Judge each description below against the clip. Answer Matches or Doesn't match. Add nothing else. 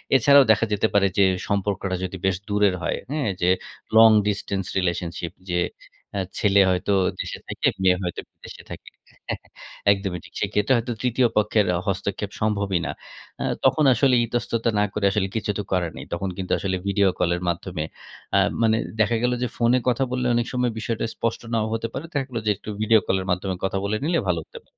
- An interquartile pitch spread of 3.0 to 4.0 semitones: Matches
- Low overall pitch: Matches